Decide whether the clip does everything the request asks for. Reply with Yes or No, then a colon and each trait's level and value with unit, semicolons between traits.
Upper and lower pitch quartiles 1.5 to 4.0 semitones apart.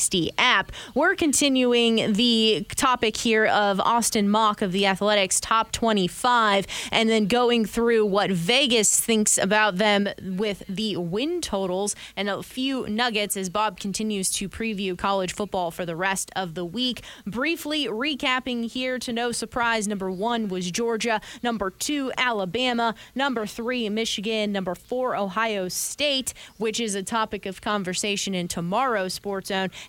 Yes: average, 3.2 semitones